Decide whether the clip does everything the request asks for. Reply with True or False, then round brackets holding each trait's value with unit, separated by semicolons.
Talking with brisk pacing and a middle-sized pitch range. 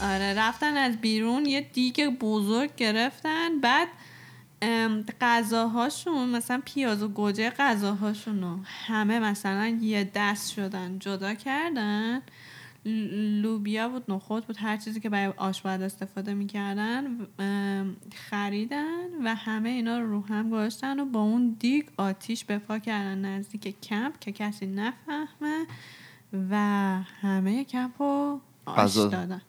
False (120 wpm; 3.4 semitones)